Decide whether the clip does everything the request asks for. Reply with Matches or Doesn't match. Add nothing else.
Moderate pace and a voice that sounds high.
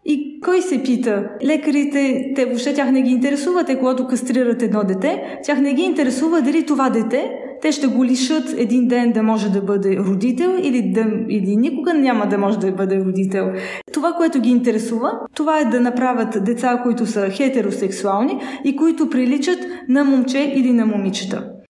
Doesn't match